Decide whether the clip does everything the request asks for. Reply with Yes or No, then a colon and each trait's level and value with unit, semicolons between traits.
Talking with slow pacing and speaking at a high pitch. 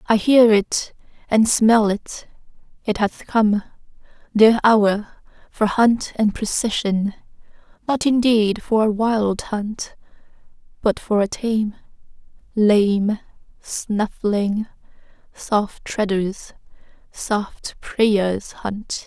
Yes: slow, 100 wpm; high, 215 Hz